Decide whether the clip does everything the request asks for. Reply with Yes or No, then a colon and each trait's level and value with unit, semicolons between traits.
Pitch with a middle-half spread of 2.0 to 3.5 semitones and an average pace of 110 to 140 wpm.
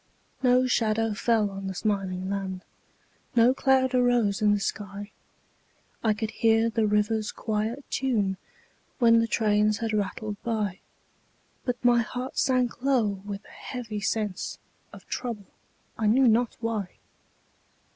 Yes: average, 2.7 semitones; slow, 135 wpm